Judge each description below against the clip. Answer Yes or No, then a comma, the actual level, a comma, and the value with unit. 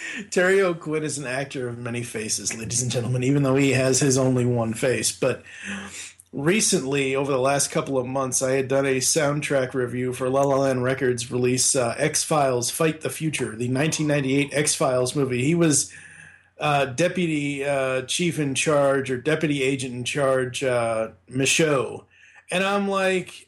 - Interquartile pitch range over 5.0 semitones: No, average, 3.1 semitones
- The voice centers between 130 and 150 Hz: Yes, low, 135 Hz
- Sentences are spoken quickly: No, average, 175 wpm